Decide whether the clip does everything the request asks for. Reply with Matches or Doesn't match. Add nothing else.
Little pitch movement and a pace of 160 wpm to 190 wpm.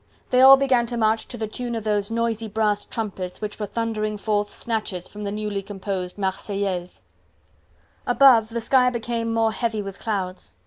Matches